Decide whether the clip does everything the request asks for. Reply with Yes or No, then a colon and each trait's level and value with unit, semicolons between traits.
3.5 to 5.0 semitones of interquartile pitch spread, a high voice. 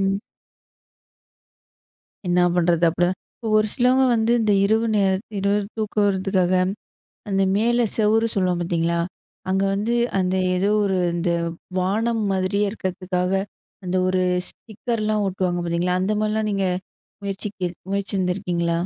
No: average, 2.8 semitones; high, 195 Hz